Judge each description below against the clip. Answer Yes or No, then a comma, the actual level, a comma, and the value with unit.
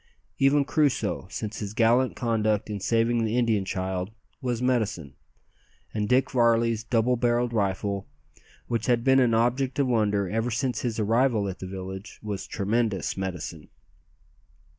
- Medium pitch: No, low, 115 Hz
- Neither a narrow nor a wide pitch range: Yes, average, 3.3 semitones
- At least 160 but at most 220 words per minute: No, average, 145 wpm